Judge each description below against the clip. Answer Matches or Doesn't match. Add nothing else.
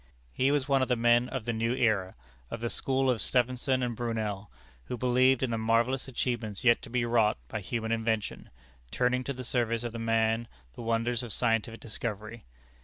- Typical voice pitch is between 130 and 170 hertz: Doesn't match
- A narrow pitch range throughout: Matches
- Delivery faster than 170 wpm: Matches